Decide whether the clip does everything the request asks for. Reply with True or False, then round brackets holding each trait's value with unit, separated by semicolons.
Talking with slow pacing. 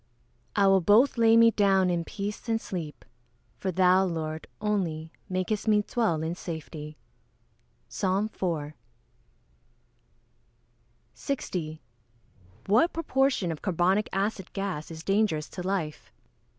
True (120 wpm)